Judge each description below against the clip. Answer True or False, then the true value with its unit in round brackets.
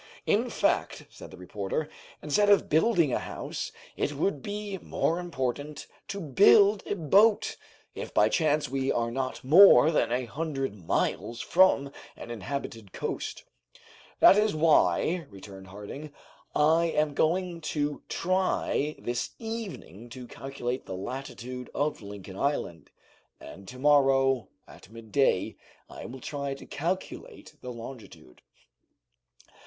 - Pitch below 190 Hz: True (140 Hz)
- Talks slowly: True (130 wpm)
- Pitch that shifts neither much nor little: False (5.8 semitones)